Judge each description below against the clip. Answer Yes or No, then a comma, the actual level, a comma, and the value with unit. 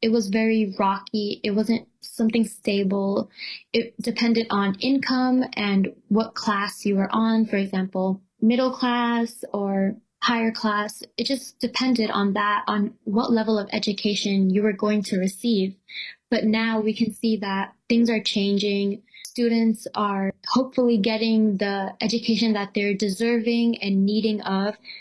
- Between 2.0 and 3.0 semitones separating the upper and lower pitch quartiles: Yes, narrow, 2.4 semitones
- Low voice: No, high, 215 Hz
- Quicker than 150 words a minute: No, average, 145 wpm